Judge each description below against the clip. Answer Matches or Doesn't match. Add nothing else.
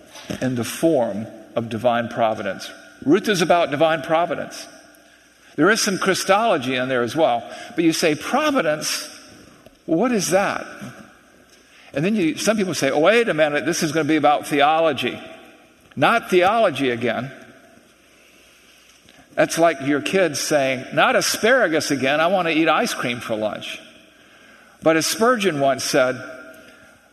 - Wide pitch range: Matches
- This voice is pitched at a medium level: Matches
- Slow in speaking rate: Doesn't match